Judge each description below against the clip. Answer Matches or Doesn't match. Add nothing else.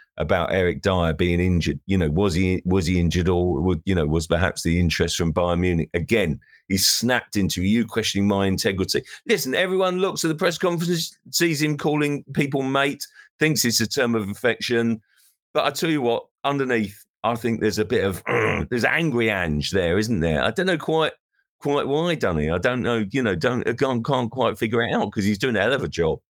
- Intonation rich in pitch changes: Matches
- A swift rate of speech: Matches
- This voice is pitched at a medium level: Doesn't match